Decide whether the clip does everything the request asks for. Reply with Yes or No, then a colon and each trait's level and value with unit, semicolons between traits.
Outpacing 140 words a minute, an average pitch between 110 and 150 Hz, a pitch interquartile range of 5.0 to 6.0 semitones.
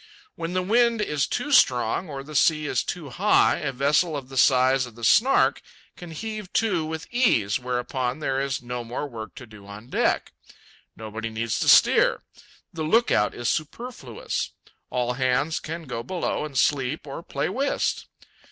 Yes: average, 170 wpm; medium, 140 Hz; wide, 5.5 semitones